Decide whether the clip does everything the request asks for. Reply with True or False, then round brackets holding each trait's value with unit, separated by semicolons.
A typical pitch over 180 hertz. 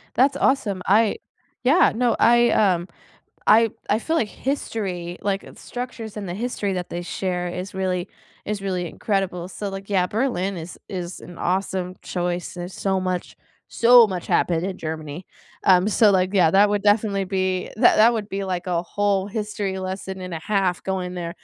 True (190 Hz)